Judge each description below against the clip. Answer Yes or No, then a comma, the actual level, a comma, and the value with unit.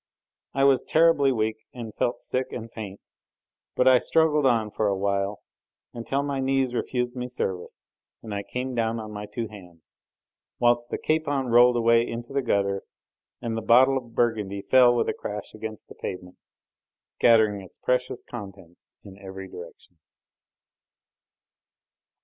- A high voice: No, low, 115 Hz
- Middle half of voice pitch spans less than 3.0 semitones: No, average, 3.8 semitones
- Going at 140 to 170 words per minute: Yes, average, 155 wpm